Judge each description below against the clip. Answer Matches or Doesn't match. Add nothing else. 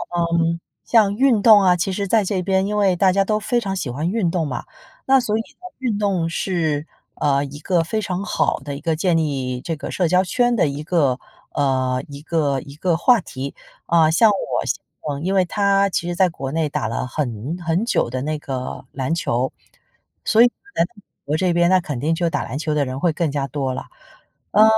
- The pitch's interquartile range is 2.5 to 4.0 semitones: Doesn't match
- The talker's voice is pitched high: Doesn't match